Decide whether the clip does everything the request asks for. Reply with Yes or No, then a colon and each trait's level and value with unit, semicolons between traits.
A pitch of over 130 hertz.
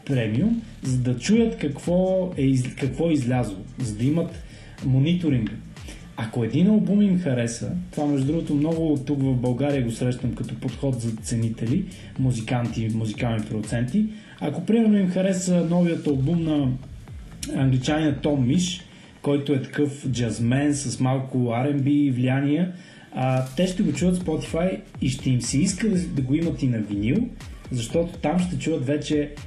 Yes: medium, 140 Hz